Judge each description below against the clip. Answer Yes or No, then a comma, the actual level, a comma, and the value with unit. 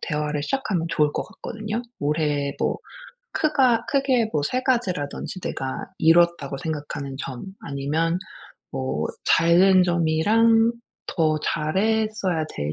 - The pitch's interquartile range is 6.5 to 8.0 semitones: Yes, wide, 6.8 semitones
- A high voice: No, medium, 165 Hz